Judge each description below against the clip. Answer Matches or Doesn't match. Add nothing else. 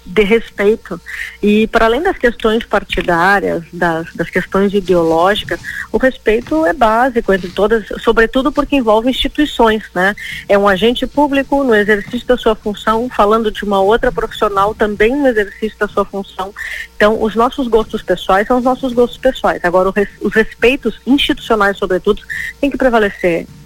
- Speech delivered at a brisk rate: Doesn't match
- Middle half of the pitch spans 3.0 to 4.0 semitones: Matches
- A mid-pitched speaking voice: Doesn't match